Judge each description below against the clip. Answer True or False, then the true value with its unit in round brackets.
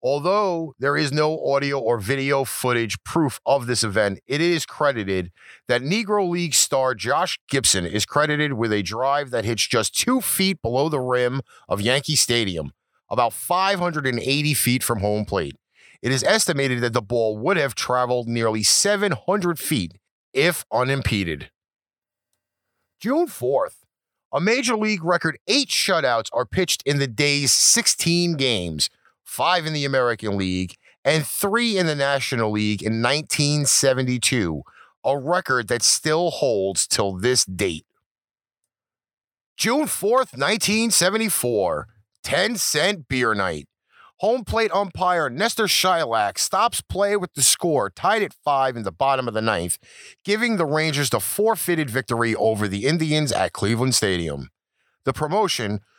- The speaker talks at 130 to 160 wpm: True (145 wpm)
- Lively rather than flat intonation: True (6.9 semitones)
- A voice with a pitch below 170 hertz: True (140 Hz)